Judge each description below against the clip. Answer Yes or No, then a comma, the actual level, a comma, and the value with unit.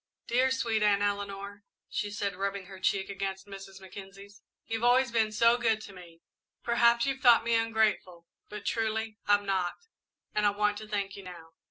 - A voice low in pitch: No, high, 205 Hz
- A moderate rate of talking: Yes, average, 180 wpm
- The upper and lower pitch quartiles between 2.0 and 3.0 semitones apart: Yes, narrow, 2.5 semitones